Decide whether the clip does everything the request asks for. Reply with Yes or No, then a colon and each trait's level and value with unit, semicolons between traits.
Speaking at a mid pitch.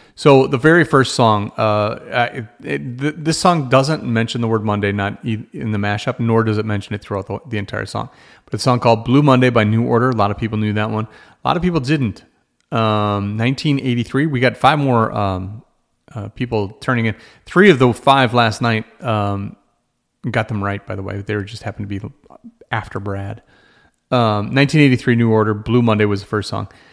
No: low, 115 Hz